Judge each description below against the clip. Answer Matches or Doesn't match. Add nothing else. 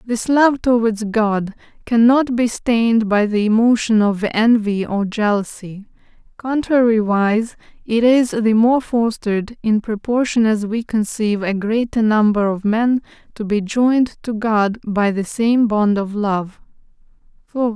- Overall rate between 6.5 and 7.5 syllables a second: Doesn't match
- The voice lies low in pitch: Doesn't match